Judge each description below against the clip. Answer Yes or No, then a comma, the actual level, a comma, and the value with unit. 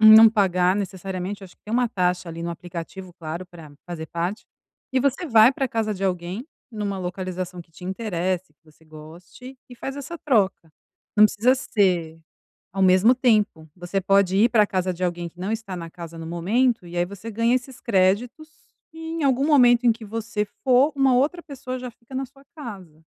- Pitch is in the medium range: No, high, 200 Hz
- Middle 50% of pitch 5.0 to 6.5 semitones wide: Yes, wide, 5.5 semitones